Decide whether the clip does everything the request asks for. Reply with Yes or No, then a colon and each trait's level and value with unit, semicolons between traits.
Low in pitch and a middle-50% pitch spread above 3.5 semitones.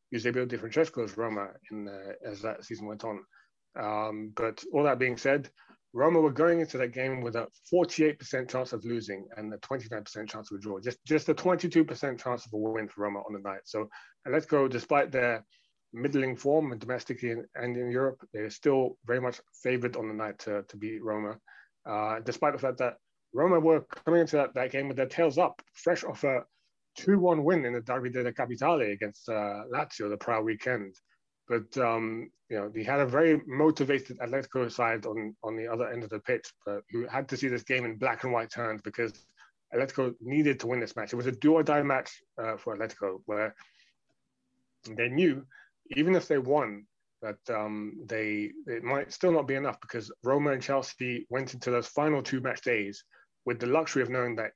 Yes: low, 125 Hz; average, 4.2 semitones